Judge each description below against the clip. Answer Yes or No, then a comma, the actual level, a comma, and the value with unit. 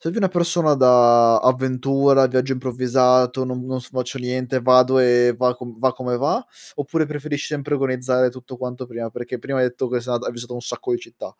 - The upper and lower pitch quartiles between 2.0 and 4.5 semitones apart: No, narrow, 1.6 semitones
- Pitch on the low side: Yes, low, 130 Hz